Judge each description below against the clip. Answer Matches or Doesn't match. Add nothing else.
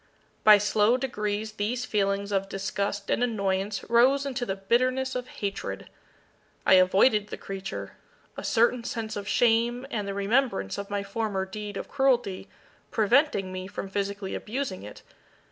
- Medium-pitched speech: Doesn't match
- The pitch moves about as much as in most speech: Matches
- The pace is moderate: Matches